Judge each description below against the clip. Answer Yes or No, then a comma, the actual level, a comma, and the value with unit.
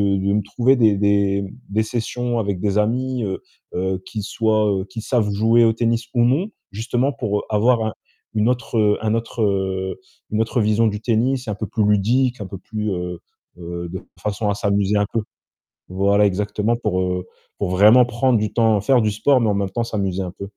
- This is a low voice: Yes, low, 105 Hz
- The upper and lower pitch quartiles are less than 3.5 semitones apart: Yes, average, 2.8 semitones